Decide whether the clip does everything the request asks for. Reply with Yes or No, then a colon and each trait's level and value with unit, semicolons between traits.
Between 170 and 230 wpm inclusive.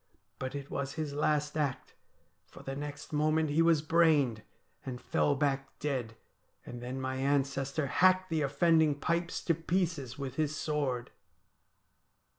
No: average, 145 wpm